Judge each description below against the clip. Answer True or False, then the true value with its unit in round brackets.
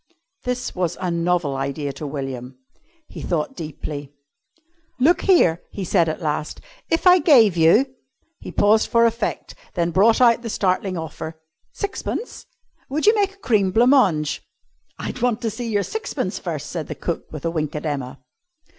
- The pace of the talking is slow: False (165 wpm)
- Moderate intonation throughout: False (7.9 semitones)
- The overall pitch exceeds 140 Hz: True (185 Hz)